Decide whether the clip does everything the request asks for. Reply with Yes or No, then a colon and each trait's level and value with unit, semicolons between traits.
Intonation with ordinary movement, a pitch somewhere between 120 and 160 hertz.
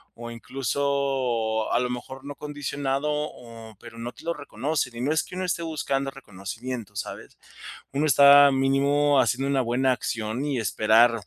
Yes: average, 3.3 semitones; low, 135 Hz